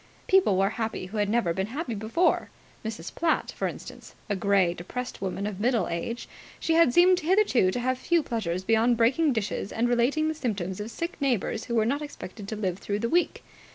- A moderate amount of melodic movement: No, wide, 5.7 semitones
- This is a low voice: No, high, 230 Hz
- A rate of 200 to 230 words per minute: Yes, fast, 205 wpm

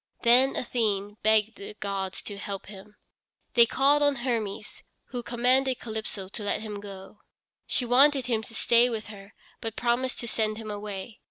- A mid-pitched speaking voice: No, high, 220 Hz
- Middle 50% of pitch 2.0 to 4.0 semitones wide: Yes, average, 3.1 semitones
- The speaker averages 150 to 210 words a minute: Yes, average, 170 wpm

